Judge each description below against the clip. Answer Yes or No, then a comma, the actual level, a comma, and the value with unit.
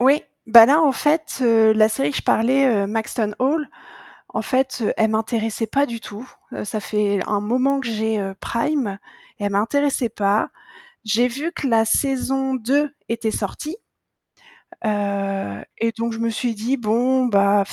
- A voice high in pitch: Yes, high, 230 Hz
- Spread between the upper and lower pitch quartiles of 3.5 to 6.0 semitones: Yes, average, 3.8 semitones